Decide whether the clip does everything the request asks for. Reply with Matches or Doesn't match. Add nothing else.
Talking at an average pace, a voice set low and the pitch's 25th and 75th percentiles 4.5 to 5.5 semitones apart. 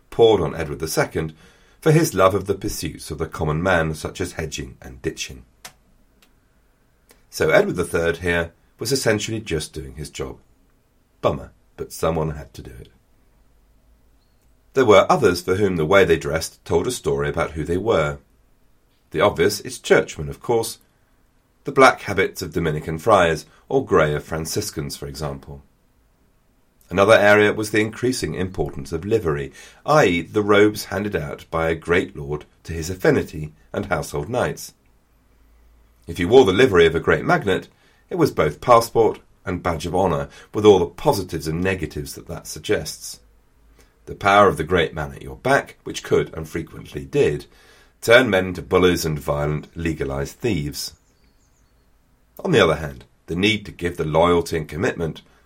Matches